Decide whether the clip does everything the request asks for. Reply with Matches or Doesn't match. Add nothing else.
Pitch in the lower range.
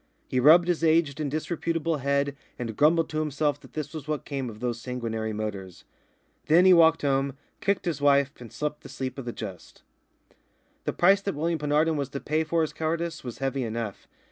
Doesn't match